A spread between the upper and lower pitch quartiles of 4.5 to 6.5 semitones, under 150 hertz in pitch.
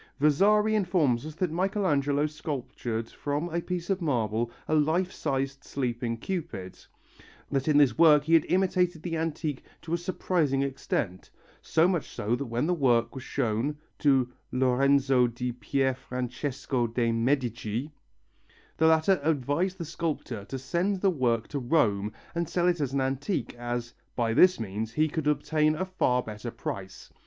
Yes: average, 5.2 semitones; medium, 140 Hz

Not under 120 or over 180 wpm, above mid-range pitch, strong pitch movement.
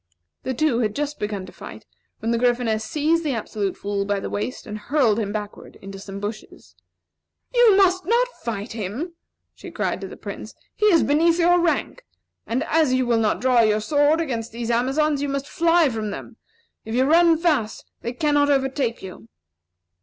No: average, 190 wpm; very high, 255 Hz; wide, 6.2 semitones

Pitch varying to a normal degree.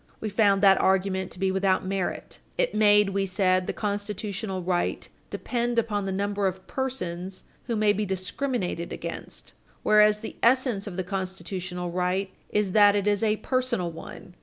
No: narrow, 2.2 semitones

